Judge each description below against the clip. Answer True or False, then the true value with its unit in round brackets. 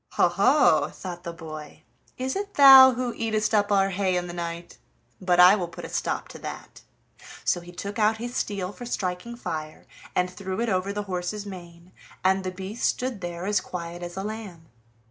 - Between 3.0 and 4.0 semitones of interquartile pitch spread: True (3.5 semitones)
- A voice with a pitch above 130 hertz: True (190 Hz)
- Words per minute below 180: False (200 wpm)